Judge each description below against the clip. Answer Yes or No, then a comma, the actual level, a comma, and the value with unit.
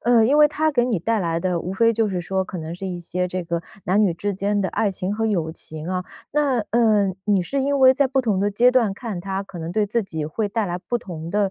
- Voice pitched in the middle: No, high, 200 Hz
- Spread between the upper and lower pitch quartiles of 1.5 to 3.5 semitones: No, average, 4.3 semitones